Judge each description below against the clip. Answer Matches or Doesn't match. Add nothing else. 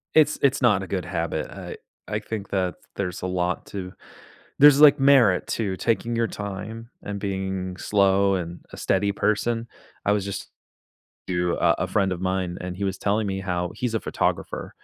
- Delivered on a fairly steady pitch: Doesn't match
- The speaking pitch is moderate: Doesn't match